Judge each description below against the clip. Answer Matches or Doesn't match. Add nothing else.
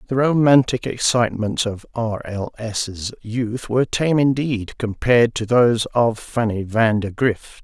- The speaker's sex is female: Doesn't match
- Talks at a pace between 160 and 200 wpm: Doesn't match